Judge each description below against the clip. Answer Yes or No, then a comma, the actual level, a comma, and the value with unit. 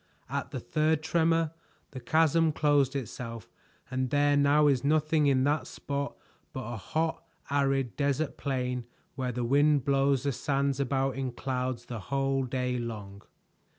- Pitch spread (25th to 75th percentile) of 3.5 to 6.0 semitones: No, narrow, 2.4 semitones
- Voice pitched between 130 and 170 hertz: Yes, low, 135 Hz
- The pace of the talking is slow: No, average, 150 wpm